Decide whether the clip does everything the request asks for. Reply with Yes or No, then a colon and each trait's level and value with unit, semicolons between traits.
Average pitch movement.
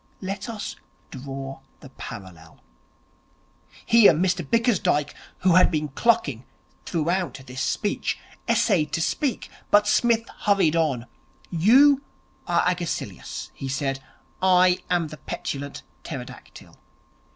No: wide, 6.6 semitones